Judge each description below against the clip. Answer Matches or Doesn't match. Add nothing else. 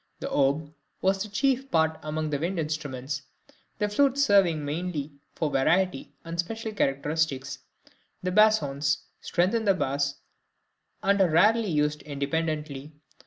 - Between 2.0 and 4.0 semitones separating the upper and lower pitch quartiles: Doesn't match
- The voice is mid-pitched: Matches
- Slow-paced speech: Matches